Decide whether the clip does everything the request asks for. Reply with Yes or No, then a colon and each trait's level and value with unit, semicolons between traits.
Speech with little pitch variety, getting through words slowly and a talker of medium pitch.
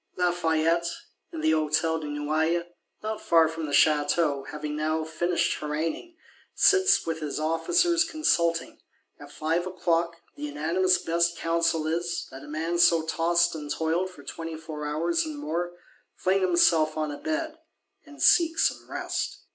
No: narrow, 1.9 semitones; average, 155 wpm; medium, 165 Hz